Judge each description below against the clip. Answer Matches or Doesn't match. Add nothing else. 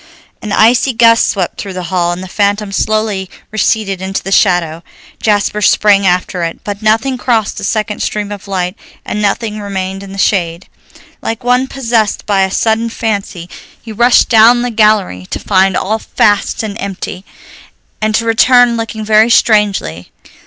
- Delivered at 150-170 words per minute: Matches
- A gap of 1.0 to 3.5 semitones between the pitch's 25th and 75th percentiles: Matches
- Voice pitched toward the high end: Matches